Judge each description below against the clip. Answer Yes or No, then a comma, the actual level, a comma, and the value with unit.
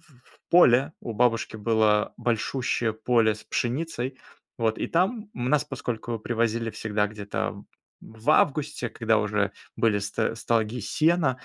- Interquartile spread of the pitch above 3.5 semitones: No, average, 3.1 semitones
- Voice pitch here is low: Yes, low, 115 Hz